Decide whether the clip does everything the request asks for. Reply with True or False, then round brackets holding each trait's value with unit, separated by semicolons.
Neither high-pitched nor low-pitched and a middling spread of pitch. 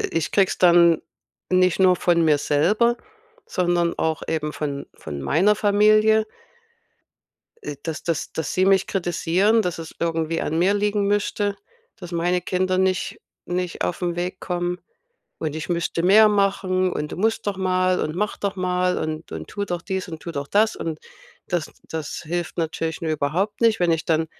True (180 Hz; 3.1 semitones)